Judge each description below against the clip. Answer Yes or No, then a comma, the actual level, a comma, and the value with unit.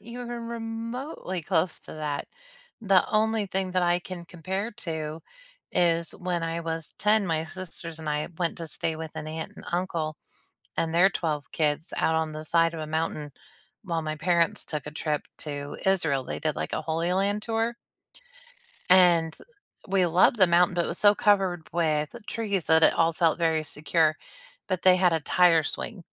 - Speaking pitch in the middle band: Yes, medium, 170 Hz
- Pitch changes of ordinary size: Yes, average, 3.0 semitones